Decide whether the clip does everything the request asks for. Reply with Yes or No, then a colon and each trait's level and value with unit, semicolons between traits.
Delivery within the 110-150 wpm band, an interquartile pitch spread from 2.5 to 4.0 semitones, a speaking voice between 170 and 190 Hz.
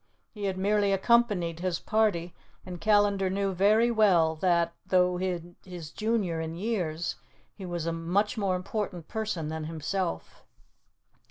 Yes: average, 140 wpm; average, 3.5 semitones; medium, 185 Hz